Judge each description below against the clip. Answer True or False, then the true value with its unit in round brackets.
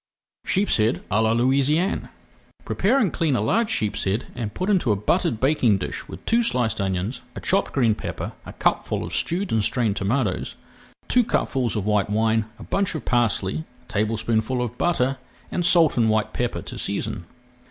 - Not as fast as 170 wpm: False (185 wpm)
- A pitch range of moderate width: False (7.2 semitones)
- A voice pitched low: True (120 Hz)